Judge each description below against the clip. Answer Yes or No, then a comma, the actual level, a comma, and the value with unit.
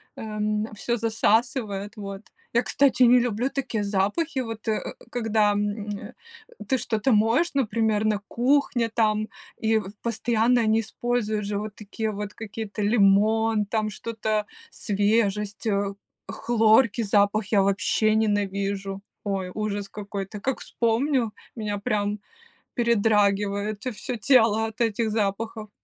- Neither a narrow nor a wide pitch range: No, narrow, 2.0 semitones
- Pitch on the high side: Yes, high, 215 Hz